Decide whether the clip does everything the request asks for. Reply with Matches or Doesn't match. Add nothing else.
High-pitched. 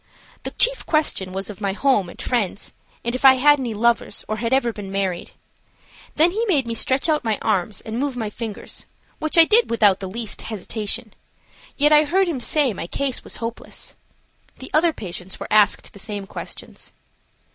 Matches